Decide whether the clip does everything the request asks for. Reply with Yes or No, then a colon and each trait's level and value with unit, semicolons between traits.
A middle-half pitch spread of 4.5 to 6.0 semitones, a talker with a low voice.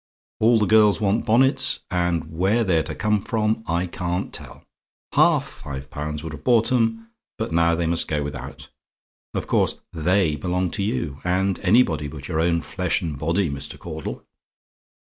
Yes: average, 5.2 semitones; very low, 90 Hz